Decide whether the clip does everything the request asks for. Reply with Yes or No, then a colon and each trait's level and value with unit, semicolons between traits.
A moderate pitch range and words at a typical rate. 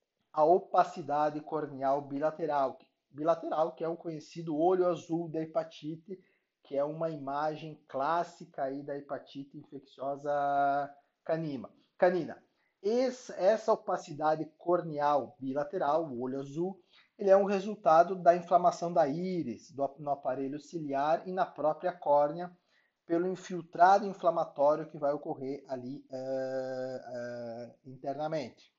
No: average, 3.8 semitones; slow, 115 wpm